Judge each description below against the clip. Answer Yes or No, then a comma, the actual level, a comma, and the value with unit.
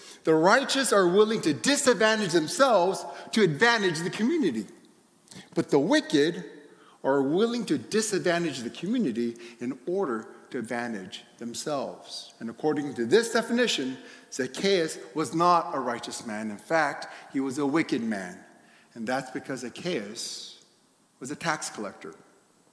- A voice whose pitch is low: No, medium, 175 Hz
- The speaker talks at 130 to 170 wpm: Yes, slow, 135 wpm